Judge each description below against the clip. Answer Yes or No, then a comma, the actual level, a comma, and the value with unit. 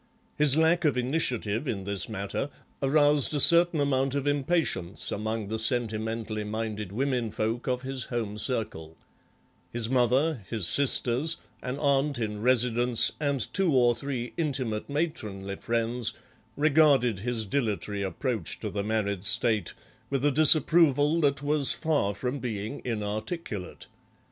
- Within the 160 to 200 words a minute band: No, slow, 135 wpm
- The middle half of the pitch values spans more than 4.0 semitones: Yes, average, 4.8 semitones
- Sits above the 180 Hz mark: No, low, 125 Hz